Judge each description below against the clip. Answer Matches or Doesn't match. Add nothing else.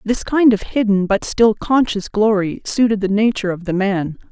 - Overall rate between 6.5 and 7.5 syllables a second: Doesn't match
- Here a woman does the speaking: Matches